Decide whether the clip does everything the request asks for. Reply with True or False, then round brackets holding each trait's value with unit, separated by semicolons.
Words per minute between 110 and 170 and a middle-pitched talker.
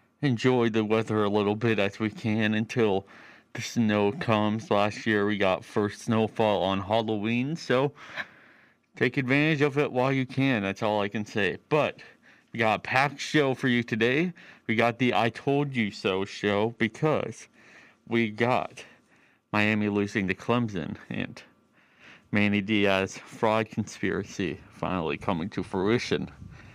False (150 wpm; 110 Hz)